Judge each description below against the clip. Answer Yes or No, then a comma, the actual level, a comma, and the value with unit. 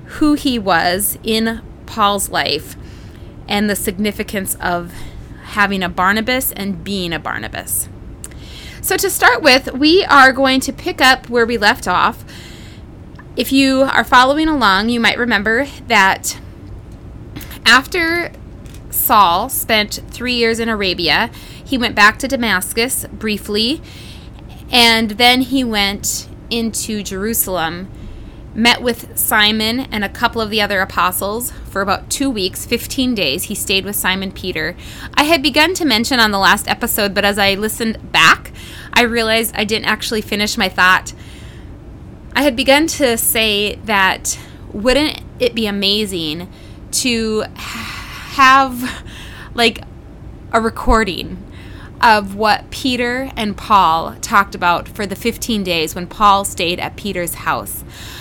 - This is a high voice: Yes, high, 220 Hz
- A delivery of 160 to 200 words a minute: No, average, 140 wpm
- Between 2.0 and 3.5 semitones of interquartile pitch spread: No, average, 4.3 semitones